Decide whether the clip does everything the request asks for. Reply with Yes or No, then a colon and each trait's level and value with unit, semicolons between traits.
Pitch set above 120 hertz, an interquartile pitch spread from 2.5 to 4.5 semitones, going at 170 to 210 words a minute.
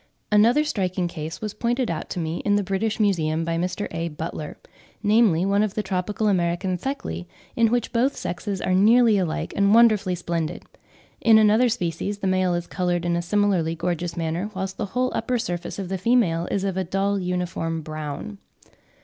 Yes: medium, 185 Hz; average, 3.7 semitones; average, 185 wpm